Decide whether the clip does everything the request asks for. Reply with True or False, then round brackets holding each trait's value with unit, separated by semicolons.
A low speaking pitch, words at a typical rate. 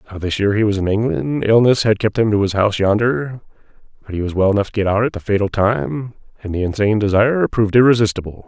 False (105 Hz; 235 wpm)